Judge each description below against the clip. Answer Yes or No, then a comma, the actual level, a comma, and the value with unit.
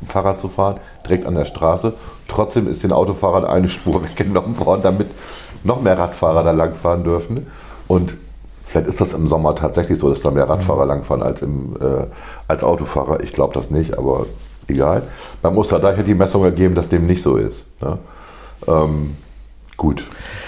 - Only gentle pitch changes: No, average, 3.5 semitones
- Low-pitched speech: Yes, very low, 90 Hz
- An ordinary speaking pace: Yes, average, 175 wpm